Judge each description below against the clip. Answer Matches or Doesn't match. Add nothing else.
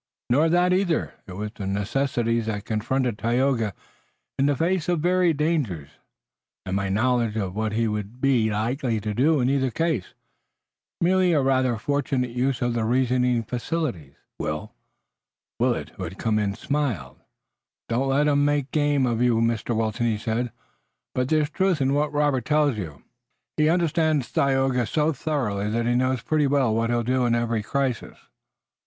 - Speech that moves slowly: Doesn't match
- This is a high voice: Doesn't match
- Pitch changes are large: Doesn't match